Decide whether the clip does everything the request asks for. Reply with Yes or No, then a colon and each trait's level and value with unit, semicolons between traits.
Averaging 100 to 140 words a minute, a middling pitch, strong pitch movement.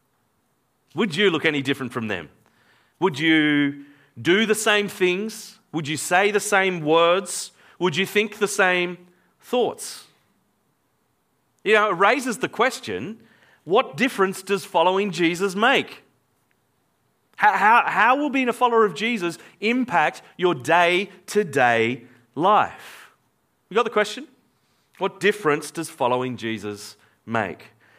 Yes: slow, 135 wpm; medium, 180 Hz; wide, 6.3 semitones